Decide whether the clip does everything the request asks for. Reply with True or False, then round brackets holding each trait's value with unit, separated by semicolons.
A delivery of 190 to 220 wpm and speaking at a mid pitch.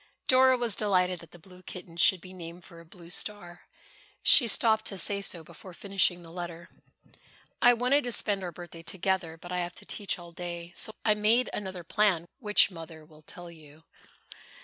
True (195 wpm; 180 Hz)